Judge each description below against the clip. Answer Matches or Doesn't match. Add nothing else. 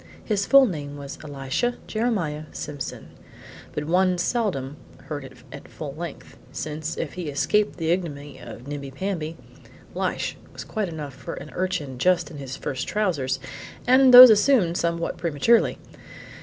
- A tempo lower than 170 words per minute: Matches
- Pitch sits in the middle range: Matches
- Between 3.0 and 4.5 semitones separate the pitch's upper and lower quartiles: Doesn't match